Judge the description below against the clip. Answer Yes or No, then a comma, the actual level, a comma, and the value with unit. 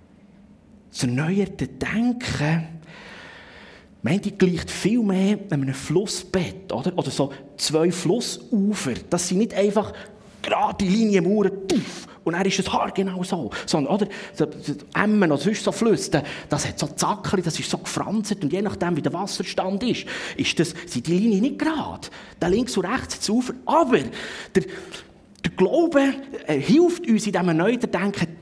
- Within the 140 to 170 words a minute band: Yes, average, 155 wpm